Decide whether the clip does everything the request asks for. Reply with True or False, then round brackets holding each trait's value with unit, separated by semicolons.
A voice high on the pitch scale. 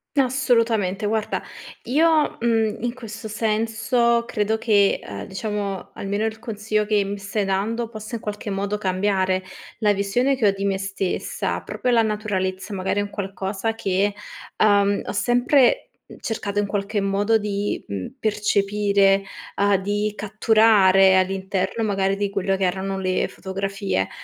True (205 Hz)